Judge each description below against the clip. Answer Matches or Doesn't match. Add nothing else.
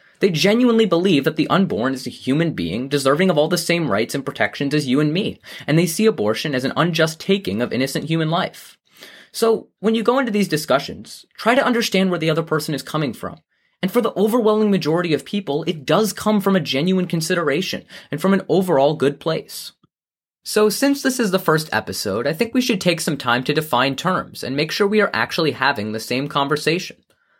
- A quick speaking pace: Matches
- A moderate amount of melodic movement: Doesn't match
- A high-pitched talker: Doesn't match